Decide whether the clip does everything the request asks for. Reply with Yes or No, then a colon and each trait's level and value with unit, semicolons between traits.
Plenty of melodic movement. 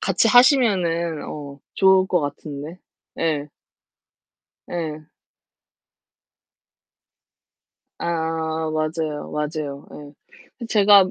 No: average, 3.7 semitones